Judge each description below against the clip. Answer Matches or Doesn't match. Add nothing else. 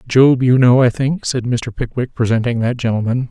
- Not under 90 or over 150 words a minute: Doesn't match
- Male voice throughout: Matches